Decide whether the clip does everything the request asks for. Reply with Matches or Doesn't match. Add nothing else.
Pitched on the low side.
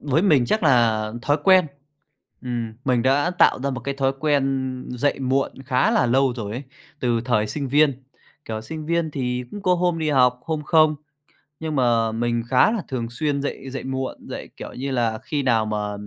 Matches